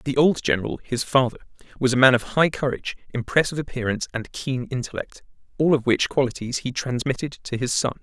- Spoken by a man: Yes, male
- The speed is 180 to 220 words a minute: Yes, average, 185 wpm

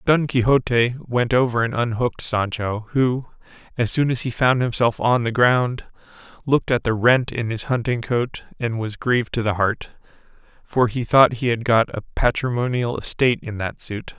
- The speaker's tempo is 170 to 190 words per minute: Yes, average, 180 wpm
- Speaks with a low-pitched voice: Yes, low, 120 Hz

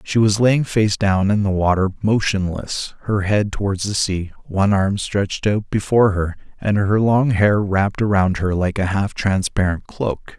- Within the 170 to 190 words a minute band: Yes, average, 185 wpm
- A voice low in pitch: Yes, low, 100 Hz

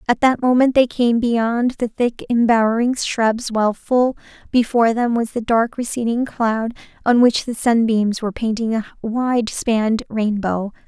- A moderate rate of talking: Yes, average, 160 wpm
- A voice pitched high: Yes, high, 230 Hz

